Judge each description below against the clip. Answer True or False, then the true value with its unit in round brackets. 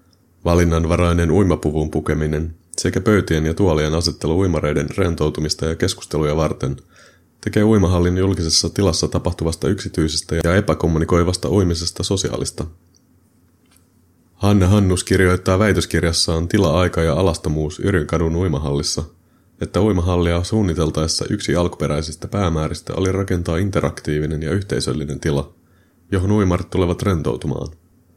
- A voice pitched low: True (85 Hz)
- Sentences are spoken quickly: False (100 wpm)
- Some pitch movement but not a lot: True (3.0 semitones)